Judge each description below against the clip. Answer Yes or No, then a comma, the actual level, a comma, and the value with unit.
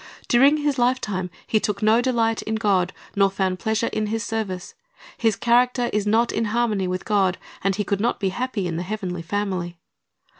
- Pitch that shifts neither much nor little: Yes, average, 3.5 semitones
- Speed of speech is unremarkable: Yes, average, 190 wpm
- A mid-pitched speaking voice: No, high, 210 Hz